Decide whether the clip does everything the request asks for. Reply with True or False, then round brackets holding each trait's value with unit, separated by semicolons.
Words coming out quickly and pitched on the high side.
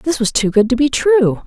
True (285 wpm; 255 Hz)